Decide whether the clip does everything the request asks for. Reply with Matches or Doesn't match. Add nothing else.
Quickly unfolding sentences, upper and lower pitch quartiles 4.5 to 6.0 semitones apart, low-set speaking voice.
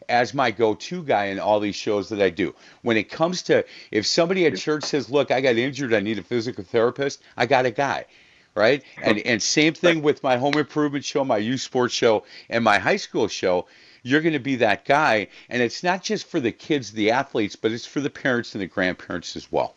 Matches